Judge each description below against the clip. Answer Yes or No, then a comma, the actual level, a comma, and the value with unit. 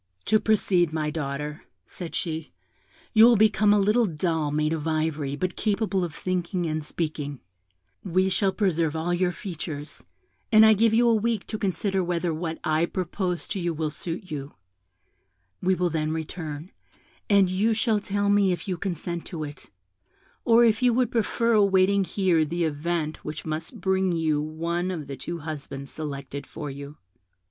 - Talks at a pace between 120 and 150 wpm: No, average, 170 wpm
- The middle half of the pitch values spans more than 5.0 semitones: No, average, 4.2 semitones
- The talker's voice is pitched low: No, medium, 175 Hz